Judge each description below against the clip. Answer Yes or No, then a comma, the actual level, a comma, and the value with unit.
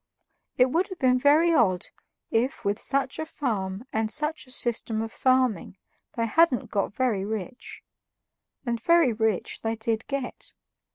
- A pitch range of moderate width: Yes, average, 3.9 semitones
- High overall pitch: Yes, high, 245 Hz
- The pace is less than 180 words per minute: Yes, average, 155 wpm